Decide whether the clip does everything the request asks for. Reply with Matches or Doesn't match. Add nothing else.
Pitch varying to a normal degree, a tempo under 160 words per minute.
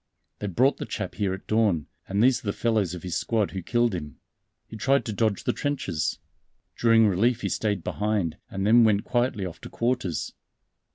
Doesn't match